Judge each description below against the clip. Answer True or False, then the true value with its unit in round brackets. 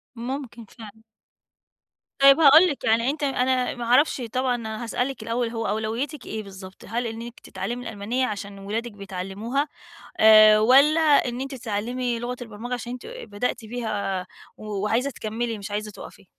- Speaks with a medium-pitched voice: False (235 Hz)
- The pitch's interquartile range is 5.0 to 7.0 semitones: False (2.9 semitones)